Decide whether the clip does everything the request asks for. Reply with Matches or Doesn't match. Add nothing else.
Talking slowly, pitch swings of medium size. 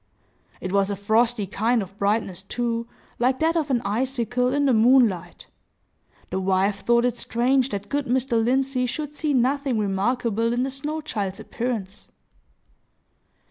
Doesn't match